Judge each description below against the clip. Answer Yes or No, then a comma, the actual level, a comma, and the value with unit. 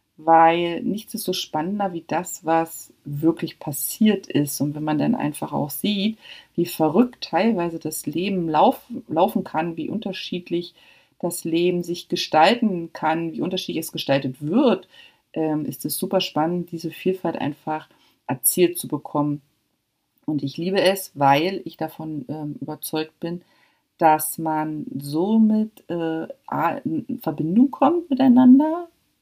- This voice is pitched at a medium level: Yes, medium, 165 Hz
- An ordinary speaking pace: Yes, average, 140 wpm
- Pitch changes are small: No, average, 3.7 semitones